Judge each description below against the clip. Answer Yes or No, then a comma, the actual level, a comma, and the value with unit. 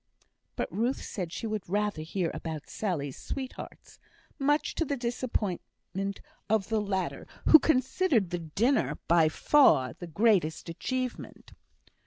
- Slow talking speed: Yes, slow, 130 wpm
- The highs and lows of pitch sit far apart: Yes, wide, 6.7 semitones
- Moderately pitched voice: No, high, 210 Hz